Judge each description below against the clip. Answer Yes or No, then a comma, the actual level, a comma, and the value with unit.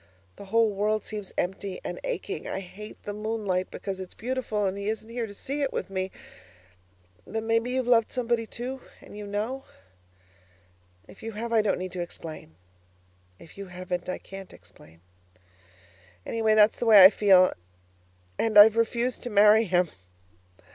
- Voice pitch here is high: Yes, high, 210 Hz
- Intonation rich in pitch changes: No, average, 3.0 semitones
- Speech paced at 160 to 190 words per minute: Yes, average, 170 wpm